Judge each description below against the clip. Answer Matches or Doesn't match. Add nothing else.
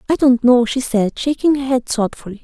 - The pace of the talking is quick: Matches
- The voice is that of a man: Doesn't match